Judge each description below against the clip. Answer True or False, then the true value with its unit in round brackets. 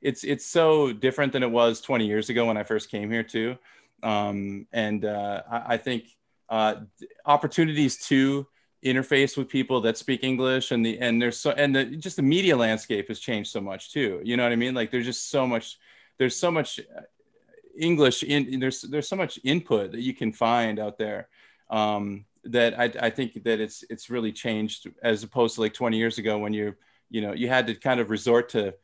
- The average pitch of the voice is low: True (120 Hz)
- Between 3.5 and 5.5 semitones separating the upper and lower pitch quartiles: False (3.1 semitones)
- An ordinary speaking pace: False (210 wpm)